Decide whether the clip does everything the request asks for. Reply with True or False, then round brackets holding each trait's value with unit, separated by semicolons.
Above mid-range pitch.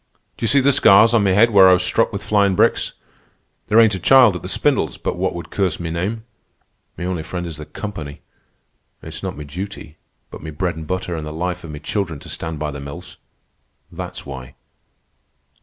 False (90 Hz)